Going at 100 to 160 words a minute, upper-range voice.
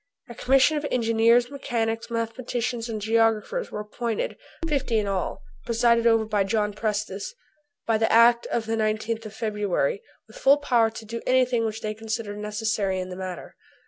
No: average, 170 wpm; high, 225 Hz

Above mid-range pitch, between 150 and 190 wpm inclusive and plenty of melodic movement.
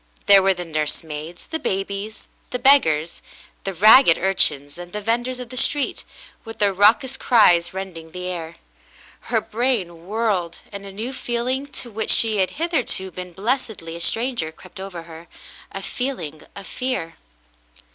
Yes: high, 195 Hz; average, 170 wpm; wide, 5.7 semitones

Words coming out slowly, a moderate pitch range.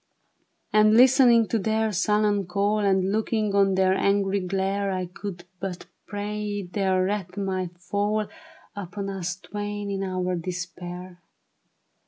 No: slow, 130 wpm; narrow, 2.1 semitones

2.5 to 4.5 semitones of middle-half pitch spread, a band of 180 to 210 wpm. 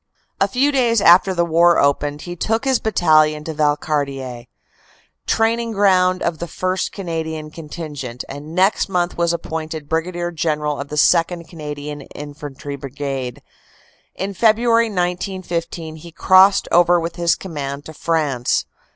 No: average, 3.7 semitones; average, 140 wpm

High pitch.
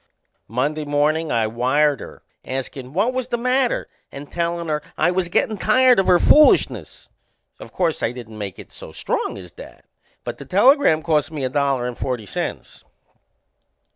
No: medium, 150 Hz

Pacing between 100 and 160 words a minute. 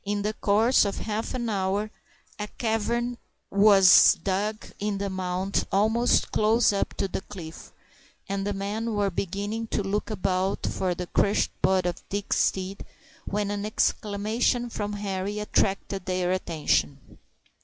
Yes: average, 145 wpm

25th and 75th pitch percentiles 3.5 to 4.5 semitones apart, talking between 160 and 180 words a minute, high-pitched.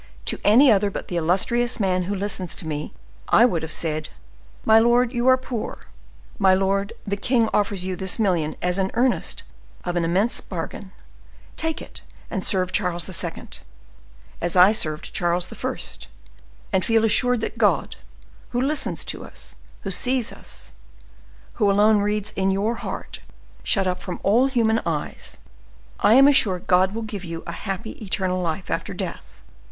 Yes: average, 4.0 semitones; average, 170 wpm; high, 195 Hz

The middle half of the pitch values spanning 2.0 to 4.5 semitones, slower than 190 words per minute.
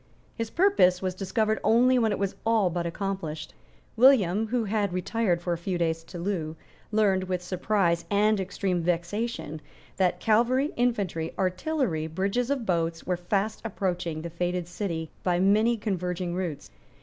Yes: average, 3.9 semitones; average, 155 wpm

